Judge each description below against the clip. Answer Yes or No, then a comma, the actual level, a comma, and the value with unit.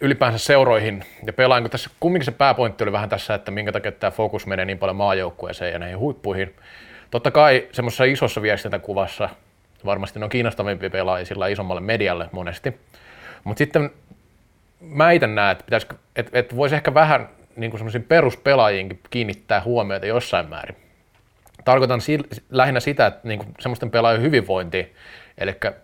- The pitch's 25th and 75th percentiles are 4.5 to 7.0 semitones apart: Yes, average, 4.8 semitones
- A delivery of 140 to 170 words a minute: Yes, fast, 155 wpm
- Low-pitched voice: Yes, low, 110 Hz